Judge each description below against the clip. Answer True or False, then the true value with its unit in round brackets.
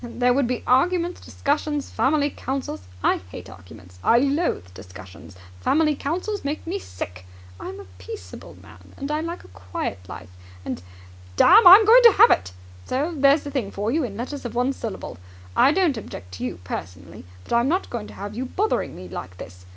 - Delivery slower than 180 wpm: False (190 wpm)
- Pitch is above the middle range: True (245 Hz)